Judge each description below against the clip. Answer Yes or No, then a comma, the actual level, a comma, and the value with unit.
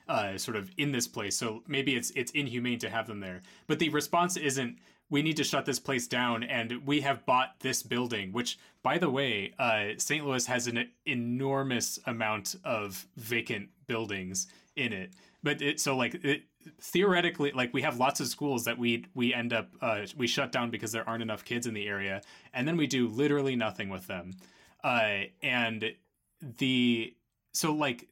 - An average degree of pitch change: Yes, average, 3.9 semitones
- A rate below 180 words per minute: No, average, 190 wpm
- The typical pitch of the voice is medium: No, low, 125 Hz